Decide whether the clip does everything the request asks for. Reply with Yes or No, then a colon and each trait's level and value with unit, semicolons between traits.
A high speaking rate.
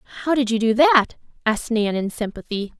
No: average, 195 wpm